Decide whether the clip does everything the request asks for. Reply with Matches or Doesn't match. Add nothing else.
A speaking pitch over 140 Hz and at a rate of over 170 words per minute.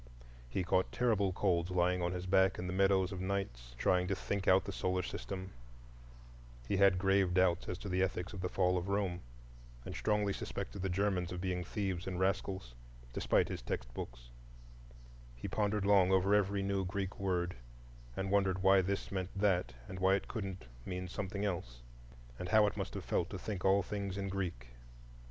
Doesn't match